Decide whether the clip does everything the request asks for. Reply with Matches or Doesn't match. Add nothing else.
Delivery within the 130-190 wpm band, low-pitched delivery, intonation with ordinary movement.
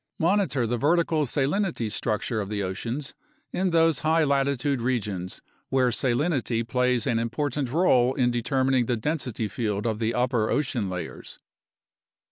Matches